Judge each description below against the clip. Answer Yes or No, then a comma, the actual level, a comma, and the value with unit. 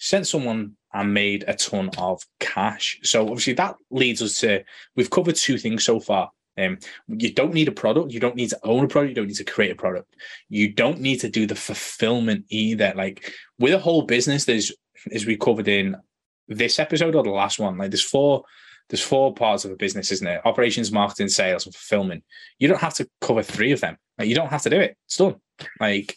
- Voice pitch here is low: Yes, low, 115 Hz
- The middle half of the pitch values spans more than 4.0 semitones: Yes, average, 4.8 semitones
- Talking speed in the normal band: No, fast, 225 wpm